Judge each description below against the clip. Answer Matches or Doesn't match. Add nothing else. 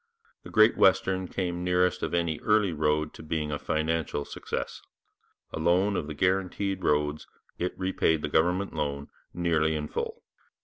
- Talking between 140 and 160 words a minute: Matches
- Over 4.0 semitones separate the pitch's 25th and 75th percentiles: Doesn't match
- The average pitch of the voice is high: Doesn't match